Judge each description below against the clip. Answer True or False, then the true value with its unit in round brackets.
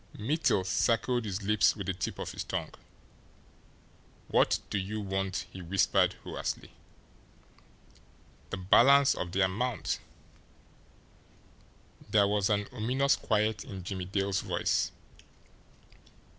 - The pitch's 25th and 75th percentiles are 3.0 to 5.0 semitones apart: False (2.6 semitones)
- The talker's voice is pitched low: True (100 Hz)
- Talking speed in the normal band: False (115 wpm)